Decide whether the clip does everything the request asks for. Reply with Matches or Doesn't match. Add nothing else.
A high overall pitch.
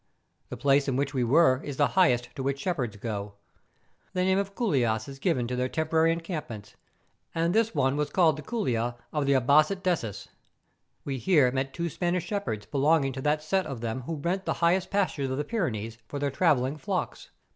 Doesn't match